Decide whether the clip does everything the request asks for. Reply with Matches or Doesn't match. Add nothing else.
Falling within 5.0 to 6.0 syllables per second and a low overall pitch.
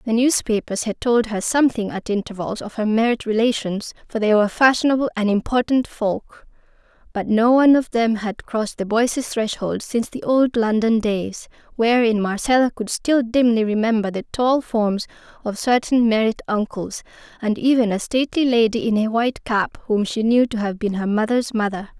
Doesn't match